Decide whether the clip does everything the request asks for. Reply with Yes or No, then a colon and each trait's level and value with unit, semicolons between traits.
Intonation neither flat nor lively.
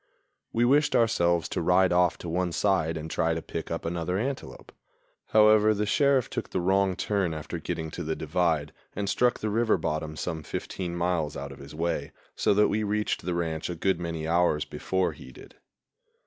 Yes: average, 4.0 semitones